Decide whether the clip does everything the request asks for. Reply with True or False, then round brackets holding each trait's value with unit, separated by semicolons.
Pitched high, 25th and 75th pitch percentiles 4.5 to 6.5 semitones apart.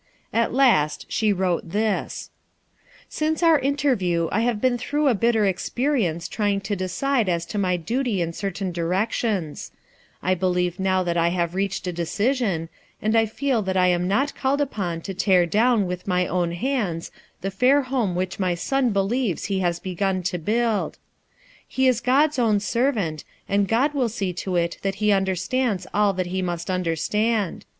True (195 Hz; 5.0 semitones)